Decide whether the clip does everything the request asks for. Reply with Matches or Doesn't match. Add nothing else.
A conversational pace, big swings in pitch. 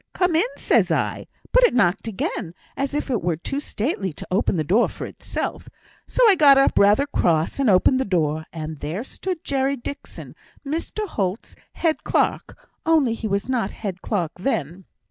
Matches